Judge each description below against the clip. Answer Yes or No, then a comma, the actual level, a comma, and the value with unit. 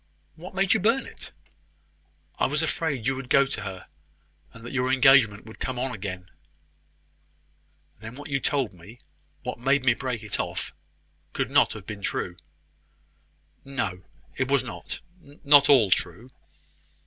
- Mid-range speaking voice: No, low, 130 Hz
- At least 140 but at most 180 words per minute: Yes, average, 155 wpm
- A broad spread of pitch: No, average, 4.7 semitones